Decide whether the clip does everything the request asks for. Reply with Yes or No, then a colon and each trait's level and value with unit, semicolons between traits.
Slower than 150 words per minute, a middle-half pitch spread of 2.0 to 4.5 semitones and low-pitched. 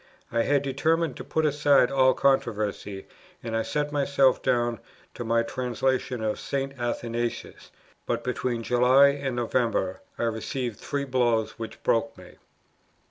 Yes: average, 140 wpm; average, 2.9 semitones; low, 125 Hz